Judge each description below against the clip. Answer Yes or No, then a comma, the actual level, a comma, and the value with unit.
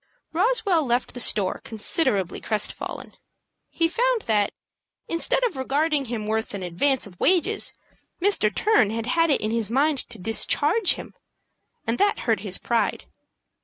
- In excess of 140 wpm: Yes, average, 155 wpm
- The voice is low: No, very high, 250 Hz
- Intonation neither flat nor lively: No, wide, 7.5 semitones